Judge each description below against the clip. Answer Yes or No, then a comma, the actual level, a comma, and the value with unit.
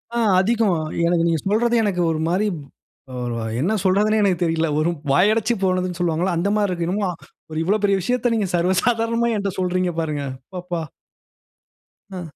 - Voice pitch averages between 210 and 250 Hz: No, medium, 185 Hz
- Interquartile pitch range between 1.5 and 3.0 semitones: No, average, 3.6 semitones